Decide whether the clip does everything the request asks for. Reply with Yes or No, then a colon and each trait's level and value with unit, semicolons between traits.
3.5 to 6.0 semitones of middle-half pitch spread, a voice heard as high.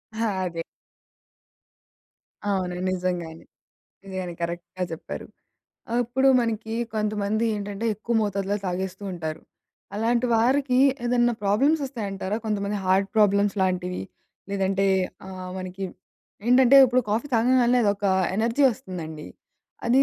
Yes: average, 3.9 semitones; high, 200 Hz